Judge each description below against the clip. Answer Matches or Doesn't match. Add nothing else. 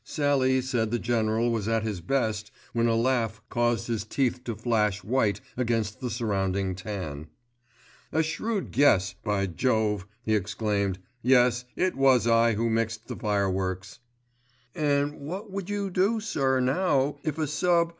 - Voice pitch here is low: Matches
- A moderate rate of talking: Matches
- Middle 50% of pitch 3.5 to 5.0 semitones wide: Matches